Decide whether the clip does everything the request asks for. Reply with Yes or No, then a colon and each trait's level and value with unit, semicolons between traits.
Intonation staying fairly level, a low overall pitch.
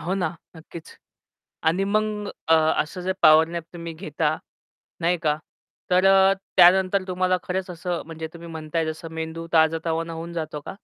No: narrow, 2.3 semitones; medium, 170 Hz